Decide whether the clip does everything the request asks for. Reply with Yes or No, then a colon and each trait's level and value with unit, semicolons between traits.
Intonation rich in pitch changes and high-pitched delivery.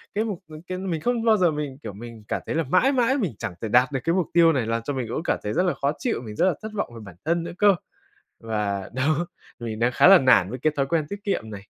No: wide, 8.0 semitones; medium, 150 Hz